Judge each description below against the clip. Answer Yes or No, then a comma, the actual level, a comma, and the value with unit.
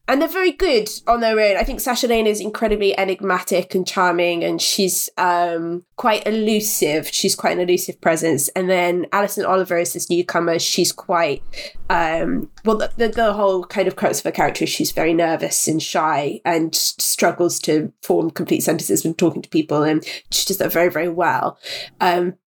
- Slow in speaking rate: No, average, 190 wpm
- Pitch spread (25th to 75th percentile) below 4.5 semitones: Yes, average, 3.6 semitones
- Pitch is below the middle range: No, medium, 185 Hz